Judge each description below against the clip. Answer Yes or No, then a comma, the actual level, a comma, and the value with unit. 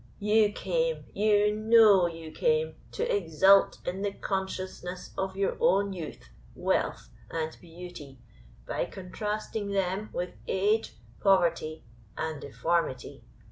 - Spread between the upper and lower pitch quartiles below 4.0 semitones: Yes, average, 3.3 semitones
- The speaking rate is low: Yes, slow, 115 wpm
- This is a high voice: Yes, high, 195 Hz